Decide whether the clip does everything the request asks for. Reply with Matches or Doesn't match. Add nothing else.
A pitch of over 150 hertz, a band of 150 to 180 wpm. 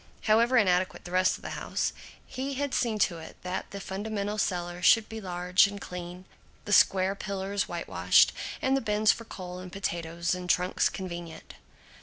Matches